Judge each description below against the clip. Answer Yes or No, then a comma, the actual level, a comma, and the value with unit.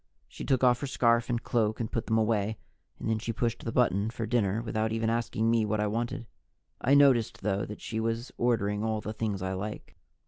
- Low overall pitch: Yes, low, 110 Hz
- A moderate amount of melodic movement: No, narrow, 1.7 semitones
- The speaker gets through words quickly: Yes, fast, 220 wpm